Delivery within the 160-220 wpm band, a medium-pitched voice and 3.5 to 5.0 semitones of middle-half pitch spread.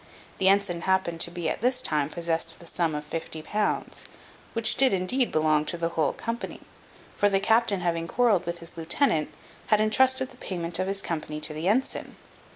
Yes: average, 195 wpm; medium, 175 Hz; average, 4.6 semitones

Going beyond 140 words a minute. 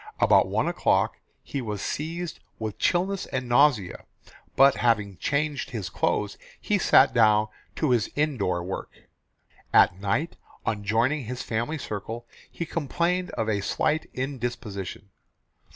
No: slow, 135 wpm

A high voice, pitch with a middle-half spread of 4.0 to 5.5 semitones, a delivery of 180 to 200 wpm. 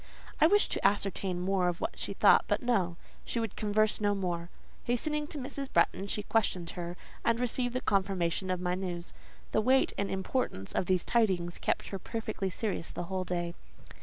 Yes: high, 195 Hz; average, 4.3 semitones; average, 190 wpm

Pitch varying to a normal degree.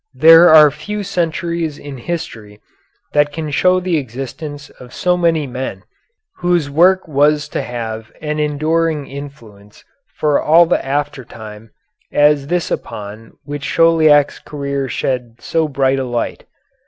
Yes: average, 3.8 semitones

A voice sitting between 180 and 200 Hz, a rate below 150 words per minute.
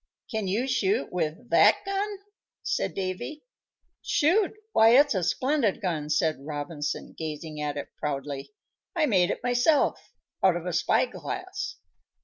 Yes: high, 190 Hz; average, 140 wpm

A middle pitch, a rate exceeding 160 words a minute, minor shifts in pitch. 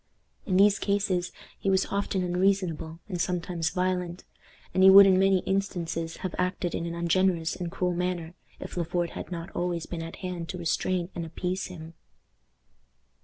Yes: medium, 180 Hz; average, 170 wpm; narrow, 1.9 semitones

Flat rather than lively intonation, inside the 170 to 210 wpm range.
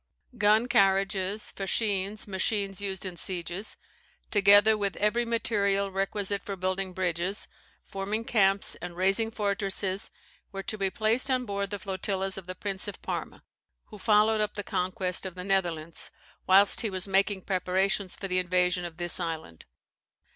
No: narrow, 1.8 semitones; average, 155 wpm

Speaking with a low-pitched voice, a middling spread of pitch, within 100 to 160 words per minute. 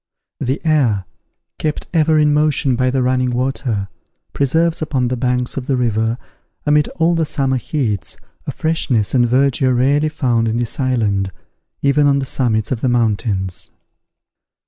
Yes: low, 130 Hz; average, 3.8 semitones; average, 155 wpm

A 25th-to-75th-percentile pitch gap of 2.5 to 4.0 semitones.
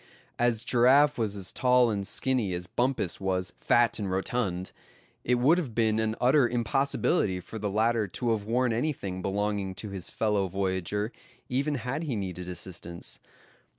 No: average, 4.5 semitones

